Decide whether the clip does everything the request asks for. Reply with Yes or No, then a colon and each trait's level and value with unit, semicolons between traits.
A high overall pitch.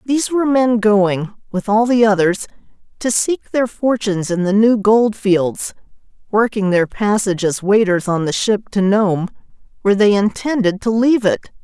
Yes: high, 210 Hz